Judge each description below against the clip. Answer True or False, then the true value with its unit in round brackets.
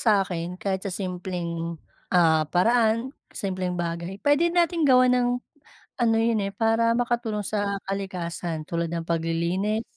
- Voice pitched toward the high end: True (195 Hz)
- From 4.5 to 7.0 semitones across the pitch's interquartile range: True (5.1 semitones)